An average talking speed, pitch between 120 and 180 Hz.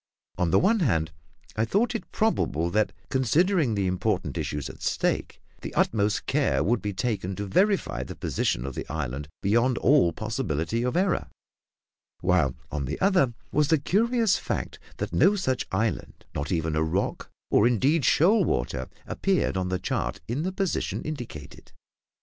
No: average, 165 wpm; low, 110 Hz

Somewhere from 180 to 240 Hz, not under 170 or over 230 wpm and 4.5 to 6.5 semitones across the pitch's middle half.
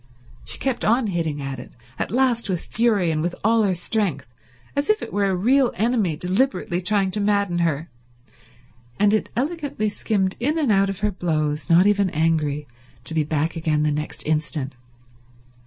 Yes: high, 190 Hz; average, 180 wpm; wide, 5.5 semitones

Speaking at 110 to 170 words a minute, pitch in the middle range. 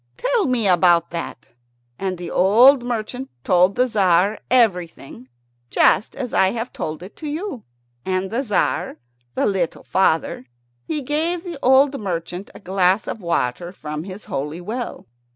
No: average, 150 wpm; high, 195 Hz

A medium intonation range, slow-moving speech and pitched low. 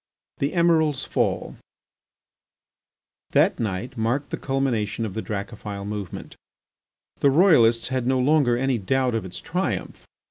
Yes: average, 4.3 semitones; slow, 130 wpm; low, 125 Hz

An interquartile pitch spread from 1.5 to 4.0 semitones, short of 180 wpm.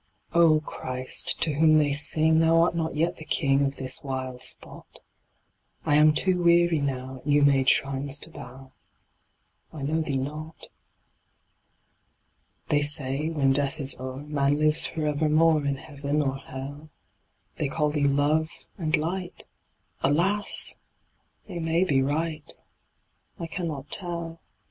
Yes: average, 2.7 semitones; average, 145 wpm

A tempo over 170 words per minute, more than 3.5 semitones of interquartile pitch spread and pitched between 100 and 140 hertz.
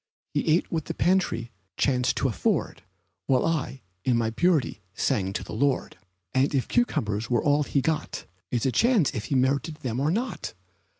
Yes: average, 180 wpm; average, 4.8 semitones; low, 135 Hz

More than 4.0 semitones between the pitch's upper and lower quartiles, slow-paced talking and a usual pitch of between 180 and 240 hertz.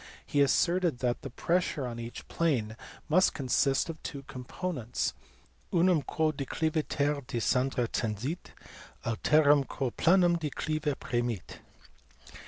No: average, 4.6 semitones; slow, 120 wpm; medium, 140 Hz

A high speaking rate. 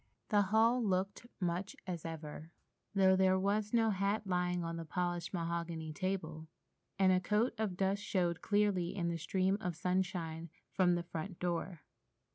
No: average, 160 wpm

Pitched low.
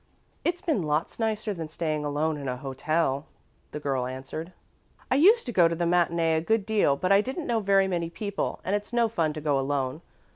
No: medium, 170 Hz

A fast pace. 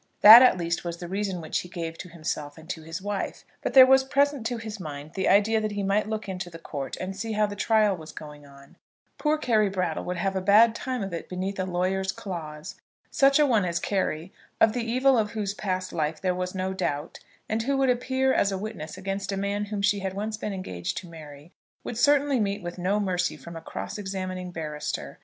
Yes: fast, 235 wpm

